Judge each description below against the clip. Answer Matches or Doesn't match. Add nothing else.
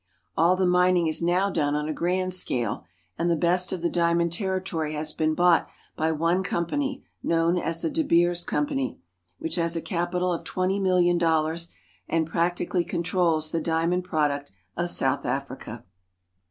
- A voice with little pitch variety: Matches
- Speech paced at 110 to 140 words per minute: Doesn't match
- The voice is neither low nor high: Matches